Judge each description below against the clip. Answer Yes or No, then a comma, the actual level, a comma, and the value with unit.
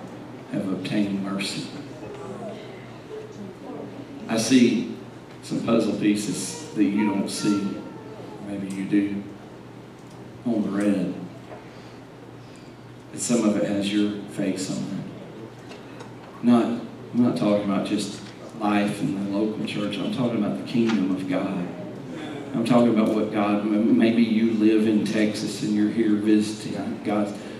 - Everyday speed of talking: No, slow, 130 wpm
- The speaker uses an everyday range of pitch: No, narrow, 1.5 semitones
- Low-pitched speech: Yes, low, 105 Hz